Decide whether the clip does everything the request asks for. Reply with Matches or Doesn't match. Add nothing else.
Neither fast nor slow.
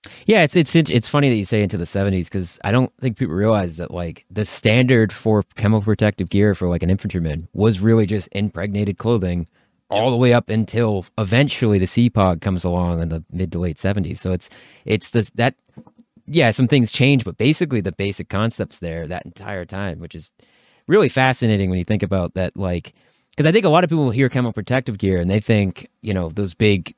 Doesn't match